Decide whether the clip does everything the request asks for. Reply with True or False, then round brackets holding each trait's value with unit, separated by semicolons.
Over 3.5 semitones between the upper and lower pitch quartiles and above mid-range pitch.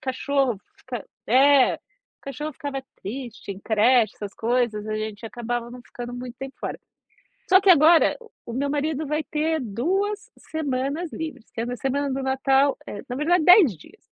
True (4.2 semitones; 265 Hz)